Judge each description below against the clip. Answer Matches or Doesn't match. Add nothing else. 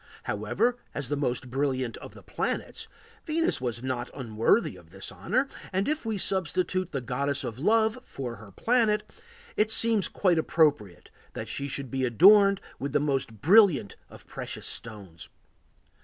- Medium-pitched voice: Matches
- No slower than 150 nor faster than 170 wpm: Matches